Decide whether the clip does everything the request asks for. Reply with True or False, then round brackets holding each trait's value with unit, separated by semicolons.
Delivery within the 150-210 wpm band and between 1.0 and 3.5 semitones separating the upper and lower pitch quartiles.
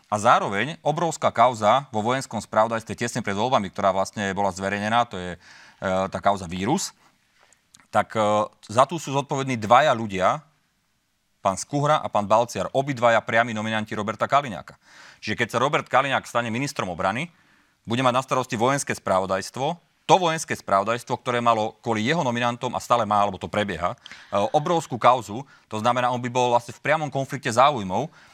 False (165 wpm; 4.1 semitones)